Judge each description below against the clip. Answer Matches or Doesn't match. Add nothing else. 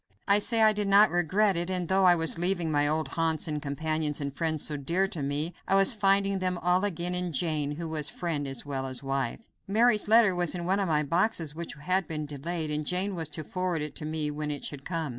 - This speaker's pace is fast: Matches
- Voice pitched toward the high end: Doesn't match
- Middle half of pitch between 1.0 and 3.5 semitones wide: Doesn't match